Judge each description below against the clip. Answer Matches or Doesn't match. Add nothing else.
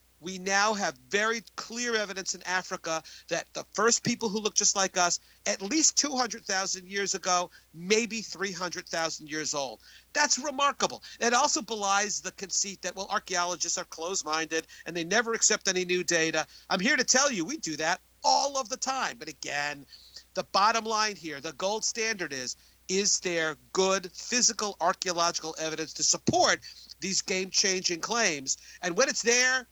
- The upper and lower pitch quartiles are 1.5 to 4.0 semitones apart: Doesn't match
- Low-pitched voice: Doesn't match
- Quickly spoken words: Doesn't match